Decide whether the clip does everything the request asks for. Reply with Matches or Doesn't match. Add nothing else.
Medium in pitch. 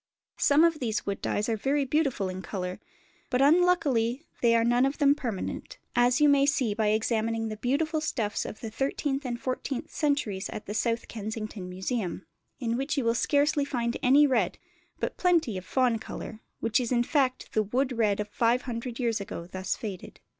Doesn't match